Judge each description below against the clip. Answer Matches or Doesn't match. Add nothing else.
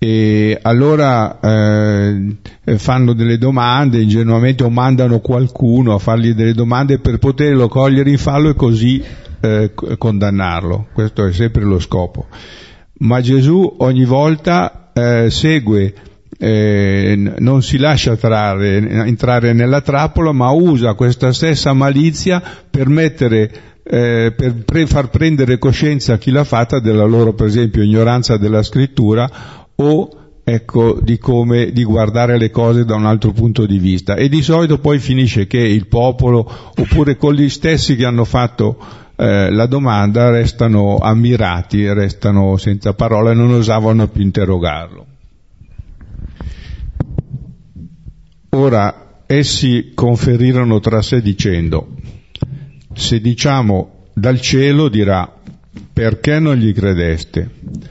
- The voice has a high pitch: Doesn't match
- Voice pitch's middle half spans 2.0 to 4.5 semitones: Matches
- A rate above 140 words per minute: Doesn't match